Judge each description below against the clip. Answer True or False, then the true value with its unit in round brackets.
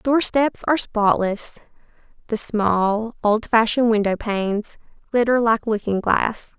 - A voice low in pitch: False (220 Hz)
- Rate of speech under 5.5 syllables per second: True (4.3 syllables/s)